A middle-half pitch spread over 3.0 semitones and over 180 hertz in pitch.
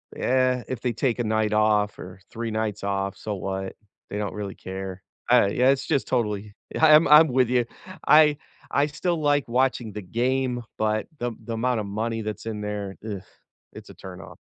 No: average, 3.7 semitones; low, 110 Hz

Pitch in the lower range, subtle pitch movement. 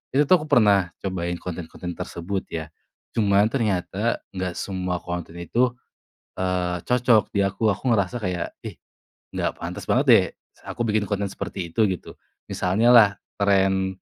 No: very low, 95 Hz; average, 3.2 semitones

